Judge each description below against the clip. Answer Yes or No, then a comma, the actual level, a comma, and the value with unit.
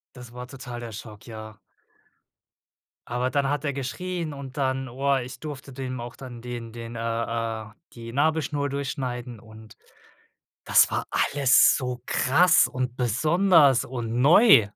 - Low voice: Yes, low, 125 Hz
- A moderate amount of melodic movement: Yes, average, 3.0 semitones